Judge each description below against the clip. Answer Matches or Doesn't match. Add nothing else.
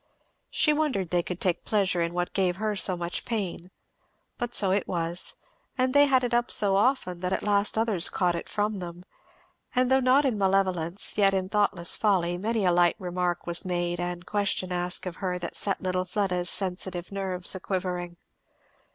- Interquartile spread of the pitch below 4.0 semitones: Matches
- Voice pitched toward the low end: Doesn't match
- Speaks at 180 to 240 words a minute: Matches